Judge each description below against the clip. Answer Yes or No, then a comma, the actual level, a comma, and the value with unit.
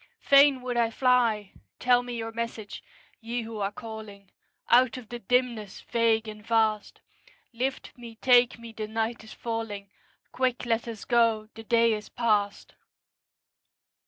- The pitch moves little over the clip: Yes, narrow, 1.9 semitones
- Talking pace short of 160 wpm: Yes, average, 150 wpm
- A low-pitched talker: No, high, 230 Hz